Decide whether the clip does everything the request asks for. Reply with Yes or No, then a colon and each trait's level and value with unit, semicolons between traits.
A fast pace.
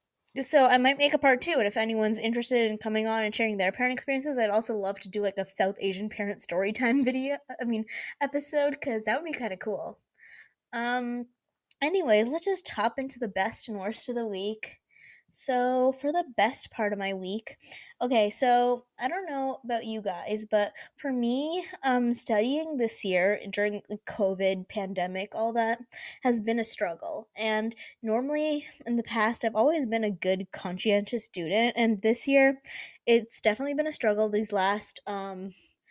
No: average, 185 wpm